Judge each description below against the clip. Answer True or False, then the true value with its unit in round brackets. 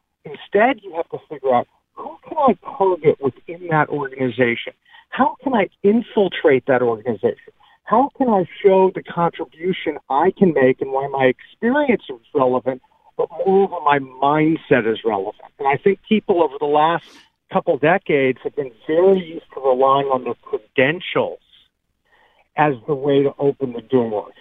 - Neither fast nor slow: True (160 wpm)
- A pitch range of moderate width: False (8.5 semitones)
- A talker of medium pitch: True (170 Hz)